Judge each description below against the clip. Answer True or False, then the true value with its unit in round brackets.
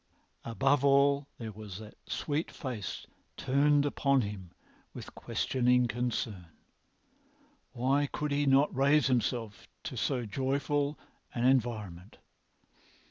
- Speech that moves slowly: True (110 wpm)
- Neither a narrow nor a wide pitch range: True (4.2 semitones)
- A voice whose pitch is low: True (130 Hz)